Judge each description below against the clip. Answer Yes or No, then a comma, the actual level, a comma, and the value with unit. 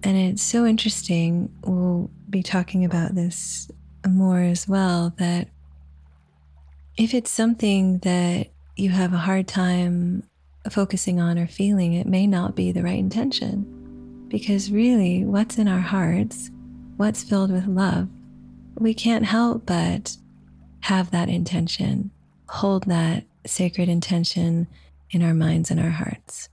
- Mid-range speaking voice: Yes, medium, 180 Hz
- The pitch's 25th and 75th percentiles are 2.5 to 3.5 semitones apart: Yes, average, 2.8 semitones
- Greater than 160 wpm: No, slow, 135 wpm